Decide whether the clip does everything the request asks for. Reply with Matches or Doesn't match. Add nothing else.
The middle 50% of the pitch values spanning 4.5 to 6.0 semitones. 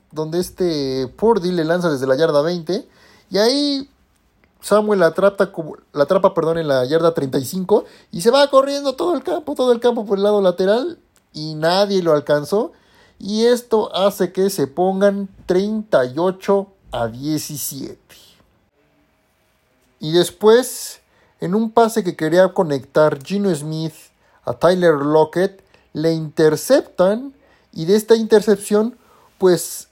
Matches